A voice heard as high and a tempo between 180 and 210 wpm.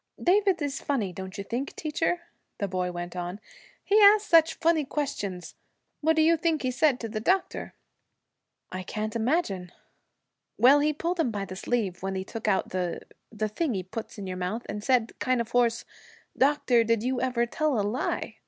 Yes: high, 235 Hz; average, 190 wpm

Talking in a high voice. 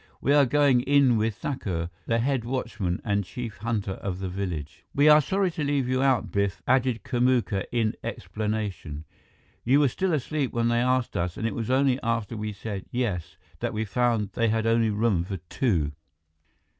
No: low, 115 Hz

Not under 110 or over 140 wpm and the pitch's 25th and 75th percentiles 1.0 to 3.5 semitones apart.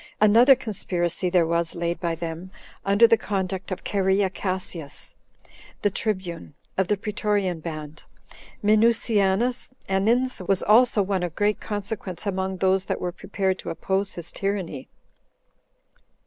Yes: slow, 135 wpm; average, 2.8 semitones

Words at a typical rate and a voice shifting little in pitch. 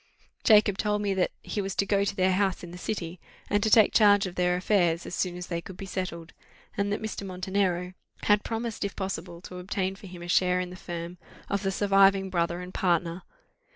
No: fast, 225 wpm; narrow, 2.1 semitones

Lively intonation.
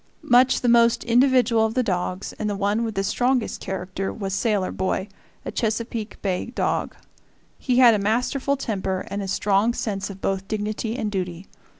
No: average, 3.5 semitones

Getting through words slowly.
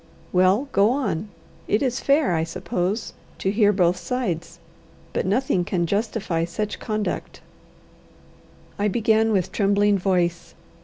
Yes: slow, 125 wpm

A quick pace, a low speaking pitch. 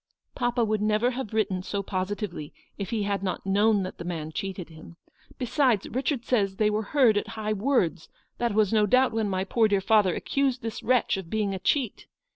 No: fast, 210 wpm; high, 210 Hz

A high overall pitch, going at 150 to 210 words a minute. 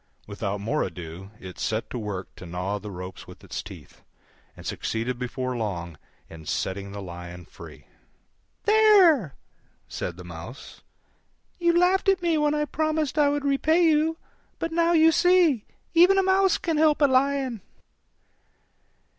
Yes: very high, 255 Hz; average, 155 wpm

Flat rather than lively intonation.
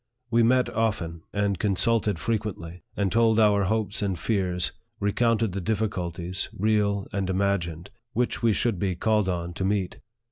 No: average, 3.2 semitones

